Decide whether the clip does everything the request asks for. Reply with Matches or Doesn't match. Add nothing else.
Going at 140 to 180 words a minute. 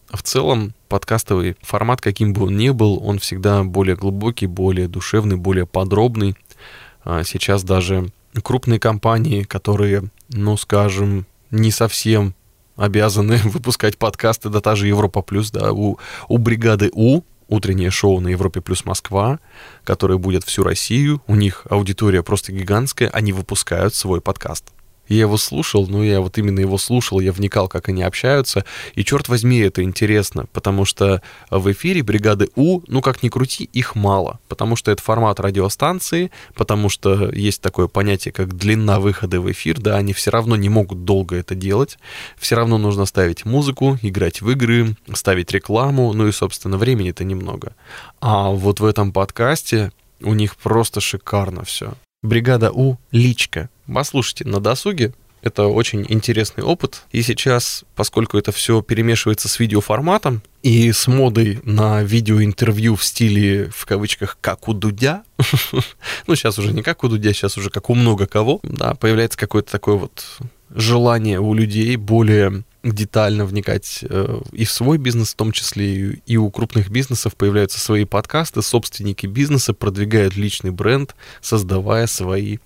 Matches